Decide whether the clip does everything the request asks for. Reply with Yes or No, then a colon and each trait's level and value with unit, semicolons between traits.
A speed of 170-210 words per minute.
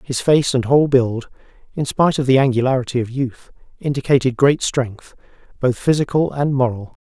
No: average, 160 wpm